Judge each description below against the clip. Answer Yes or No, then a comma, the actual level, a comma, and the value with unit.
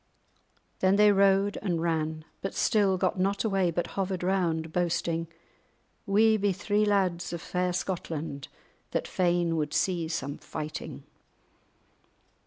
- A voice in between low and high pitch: Yes, medium, 180 Hz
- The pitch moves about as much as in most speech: Yes, average, 3.0 semitones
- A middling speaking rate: No, slow, 130 wpm